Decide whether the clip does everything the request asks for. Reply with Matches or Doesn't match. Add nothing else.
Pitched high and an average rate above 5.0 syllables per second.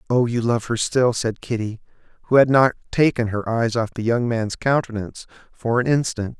Doesn't match